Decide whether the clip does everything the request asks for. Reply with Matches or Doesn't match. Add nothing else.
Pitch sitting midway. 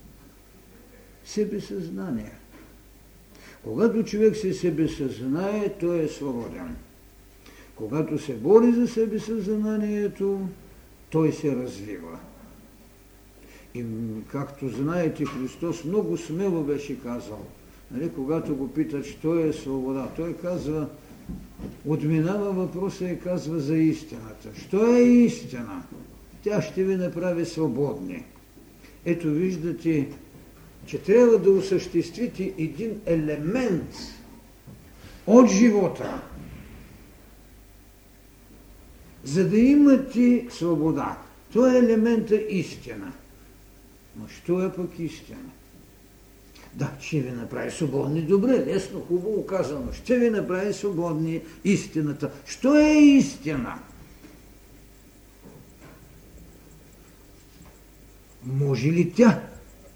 Matches